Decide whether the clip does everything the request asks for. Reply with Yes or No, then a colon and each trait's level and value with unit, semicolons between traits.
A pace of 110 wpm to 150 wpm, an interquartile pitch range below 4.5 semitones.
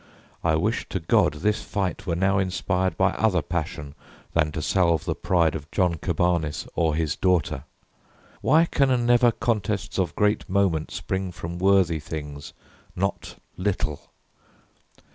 Yes: average, 145 wpm; average, 3.7 semitones